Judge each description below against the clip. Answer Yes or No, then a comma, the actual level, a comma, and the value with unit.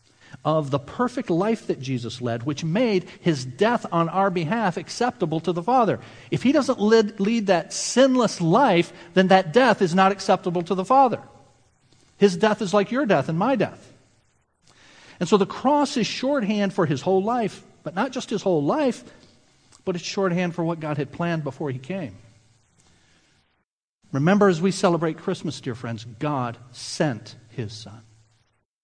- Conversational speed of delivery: Yes, average, 170 wpm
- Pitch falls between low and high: Yes, medium, 180 Hz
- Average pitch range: No, wide, 6.7 semitones